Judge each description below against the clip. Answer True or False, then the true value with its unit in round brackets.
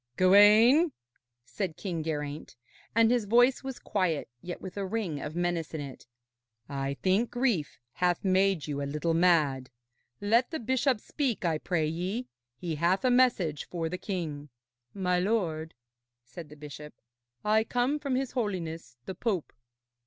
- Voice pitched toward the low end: False (180 Hz)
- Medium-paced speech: True (155 wpm)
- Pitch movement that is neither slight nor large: False (6.2 semitones)